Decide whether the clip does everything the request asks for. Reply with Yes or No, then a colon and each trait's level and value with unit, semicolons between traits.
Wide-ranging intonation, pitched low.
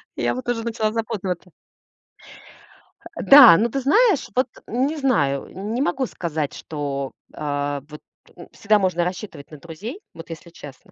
No: wide, 8.0 semitones; high, 190 Hz